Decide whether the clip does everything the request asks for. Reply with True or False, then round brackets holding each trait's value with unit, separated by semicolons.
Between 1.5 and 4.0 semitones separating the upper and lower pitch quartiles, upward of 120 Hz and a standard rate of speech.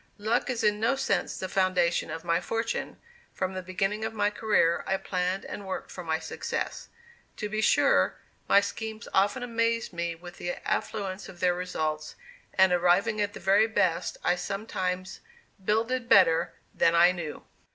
True (3.4 semitones; 190 Hz; 170 wpm)